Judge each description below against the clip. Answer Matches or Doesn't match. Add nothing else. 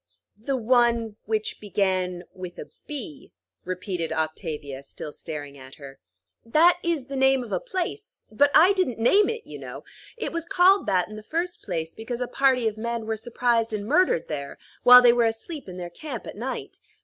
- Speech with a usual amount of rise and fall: Doesn't match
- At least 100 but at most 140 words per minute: Doesn't match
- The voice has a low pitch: Doesn't match